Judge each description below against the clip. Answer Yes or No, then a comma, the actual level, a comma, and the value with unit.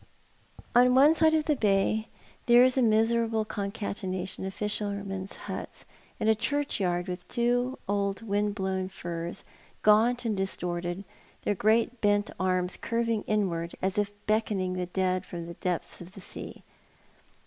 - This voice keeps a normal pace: Yes, average, 150 wpm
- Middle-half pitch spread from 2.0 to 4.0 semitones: Yes, average, 3.4 semitones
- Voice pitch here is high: Yes, high, 205 Hz